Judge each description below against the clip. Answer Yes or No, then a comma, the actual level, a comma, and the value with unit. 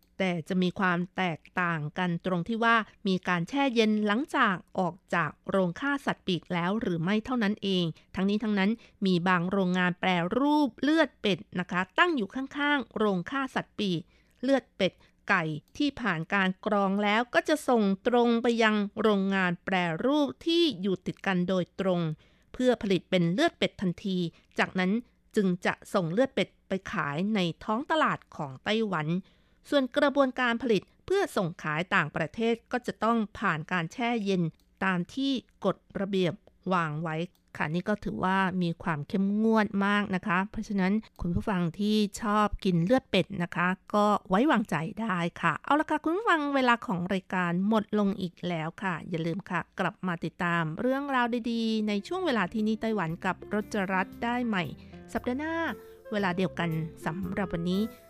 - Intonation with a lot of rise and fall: No, average, 4.3 semitones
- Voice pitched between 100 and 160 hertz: No, high, 200 Hz